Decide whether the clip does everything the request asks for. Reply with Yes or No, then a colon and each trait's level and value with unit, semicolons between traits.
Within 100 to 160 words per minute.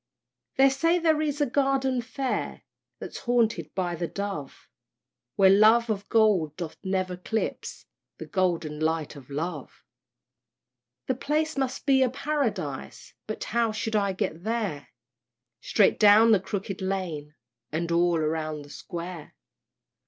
Yes: average, 140 wpm